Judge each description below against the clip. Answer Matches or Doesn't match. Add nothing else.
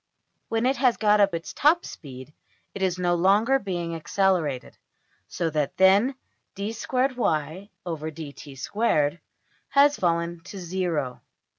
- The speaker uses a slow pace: Matches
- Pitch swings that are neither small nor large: Matches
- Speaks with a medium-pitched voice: Matches